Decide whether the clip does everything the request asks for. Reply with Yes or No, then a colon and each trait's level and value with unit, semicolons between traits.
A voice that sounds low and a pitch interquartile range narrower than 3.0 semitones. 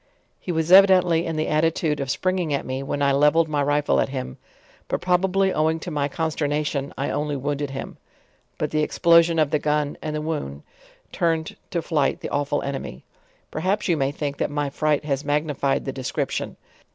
No: medium, 150 Hz; narrow, 2.5 semitones